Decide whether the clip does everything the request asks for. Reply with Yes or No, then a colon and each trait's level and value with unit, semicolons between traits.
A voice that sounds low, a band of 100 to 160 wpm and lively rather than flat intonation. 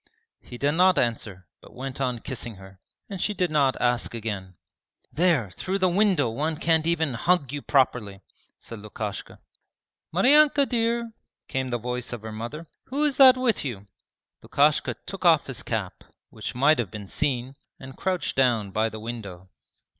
No: low, 130 Hz; average, 170 wpm; wide, 7.8 semitones